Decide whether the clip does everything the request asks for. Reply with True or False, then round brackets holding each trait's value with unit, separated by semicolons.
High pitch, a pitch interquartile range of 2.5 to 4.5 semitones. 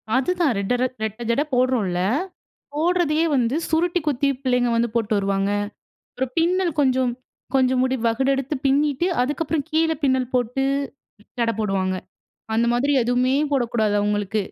True (255 Hz; 4.0 semitones)